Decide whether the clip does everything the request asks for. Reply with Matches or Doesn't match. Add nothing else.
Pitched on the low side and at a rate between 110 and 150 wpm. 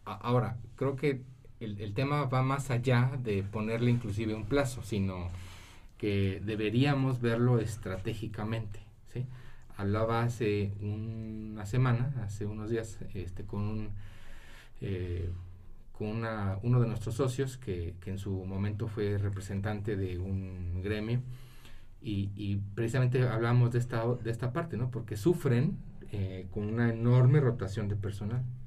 Matches